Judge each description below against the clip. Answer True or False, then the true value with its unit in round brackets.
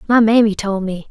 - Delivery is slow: False (215 wpm)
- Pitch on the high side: True (210 Hz)